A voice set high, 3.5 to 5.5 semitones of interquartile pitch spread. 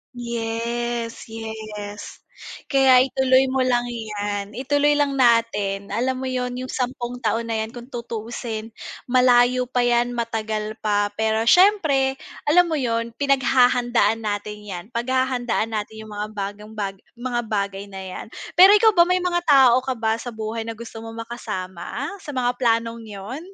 No: high, 235 Hz; average, 2.8 semitones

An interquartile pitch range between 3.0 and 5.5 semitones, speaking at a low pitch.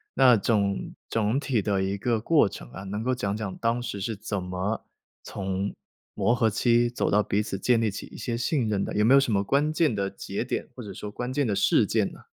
Yes: average, 3.5 semitones; low, 110 Hz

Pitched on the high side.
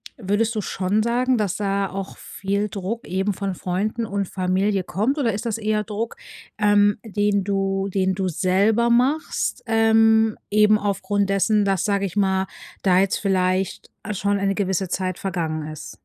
Yes: high, 200 Hz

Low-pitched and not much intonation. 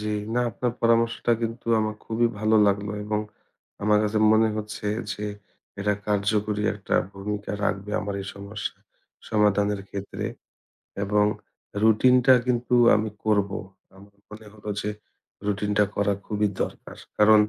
Yes: low, 105 Hz; narrow, 1.1 semitones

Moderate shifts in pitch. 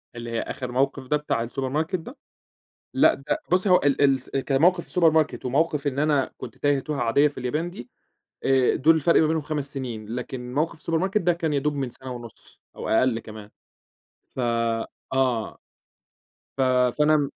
Yes: average, 3.6 semitones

